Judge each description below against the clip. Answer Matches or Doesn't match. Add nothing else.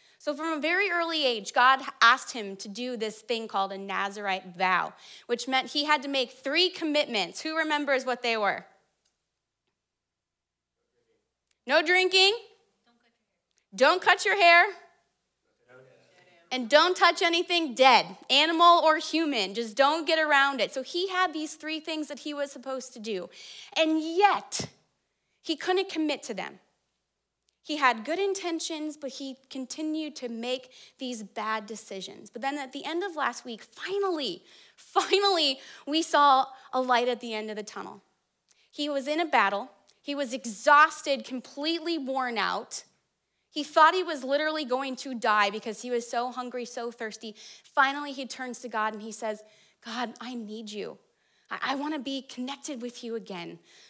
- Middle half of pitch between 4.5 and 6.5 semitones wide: Matches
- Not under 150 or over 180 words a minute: Matches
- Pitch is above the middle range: Matches